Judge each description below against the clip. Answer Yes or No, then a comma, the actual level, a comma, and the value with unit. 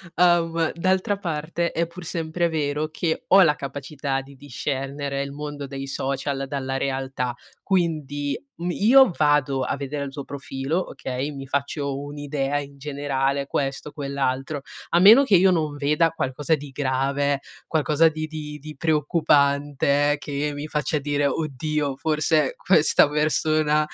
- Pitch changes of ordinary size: No, narrow, 2.2 semitones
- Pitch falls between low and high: Yes, medium, 145 Hz